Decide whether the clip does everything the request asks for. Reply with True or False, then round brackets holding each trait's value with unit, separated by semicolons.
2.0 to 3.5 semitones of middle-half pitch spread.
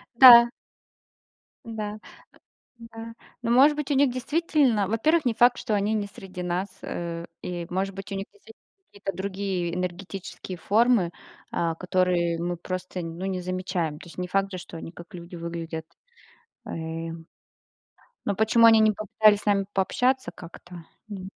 False (4.3 semitones)